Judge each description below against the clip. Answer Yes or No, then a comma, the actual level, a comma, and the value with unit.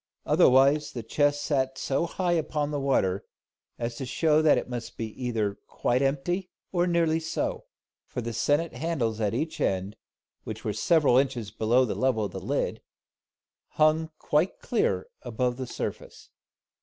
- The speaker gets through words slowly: No, average, 160 wpm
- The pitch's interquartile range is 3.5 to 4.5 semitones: No, average, 5.0 semitones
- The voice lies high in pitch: No, low, 135 Hz